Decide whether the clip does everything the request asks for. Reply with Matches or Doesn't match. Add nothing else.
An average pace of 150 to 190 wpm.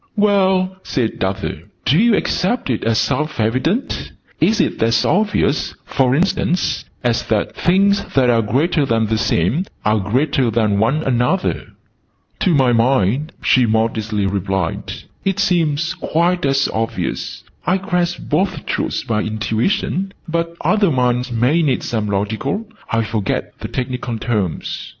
Doesn't match